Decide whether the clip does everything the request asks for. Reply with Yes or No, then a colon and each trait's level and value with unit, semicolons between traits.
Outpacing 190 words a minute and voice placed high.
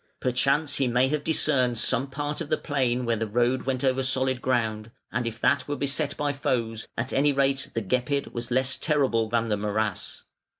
No: average, 200 wpm; low, 130 Hz